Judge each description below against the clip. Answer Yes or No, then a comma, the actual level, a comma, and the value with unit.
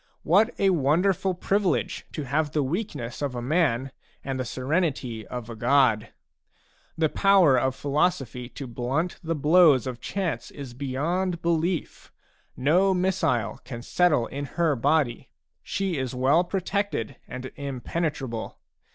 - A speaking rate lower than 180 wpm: Yes, slow, 135 wpm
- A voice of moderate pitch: Yes, medium, 145 Hz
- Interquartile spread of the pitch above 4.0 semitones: Yes, wide, 5.5 semitones